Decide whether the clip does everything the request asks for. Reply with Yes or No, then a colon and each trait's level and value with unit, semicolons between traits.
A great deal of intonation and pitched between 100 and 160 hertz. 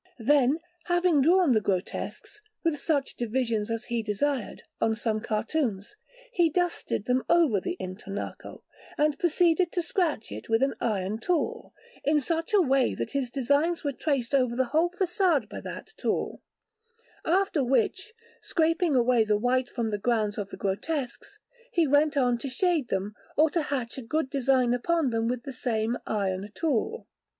No: wide, 6.2 semitones; very high, 265 Hz